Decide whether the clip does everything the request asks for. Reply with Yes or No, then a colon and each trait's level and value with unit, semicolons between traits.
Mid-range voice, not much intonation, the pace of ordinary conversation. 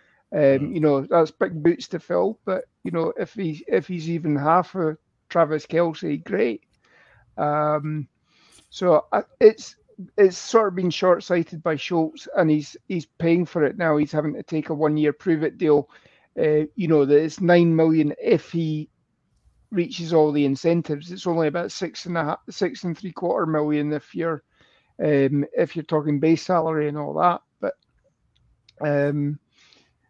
Yes: medium, 160 Hz; narrow, 2.3 semitones; average, 175 wpm